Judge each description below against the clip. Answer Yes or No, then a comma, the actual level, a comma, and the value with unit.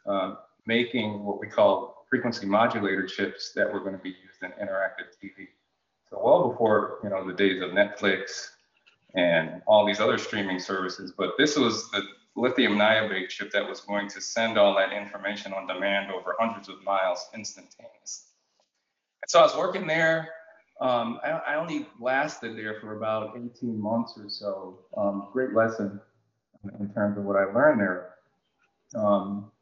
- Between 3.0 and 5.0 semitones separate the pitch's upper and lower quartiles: No, narrow, 2.6 semitones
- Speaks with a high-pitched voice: No, low, 105 Hz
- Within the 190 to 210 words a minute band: No, average, 170 wpm